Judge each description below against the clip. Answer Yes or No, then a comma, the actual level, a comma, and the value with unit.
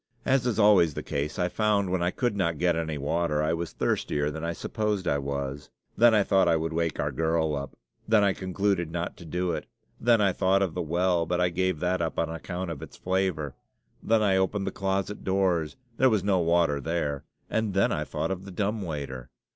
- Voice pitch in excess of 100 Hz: No, very low, 90 Hz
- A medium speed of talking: No, fast, 225 wpm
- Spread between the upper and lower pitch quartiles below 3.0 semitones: No, average, 3.3 semitones